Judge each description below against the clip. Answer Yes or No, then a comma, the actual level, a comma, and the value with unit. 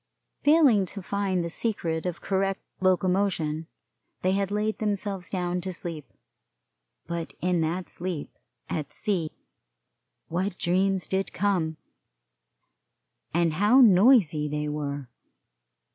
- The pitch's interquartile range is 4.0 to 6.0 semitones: No, average, 3.3 semitones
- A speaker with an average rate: No, slow, 115 wpm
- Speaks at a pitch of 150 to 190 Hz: Yes, medium, 185 Hz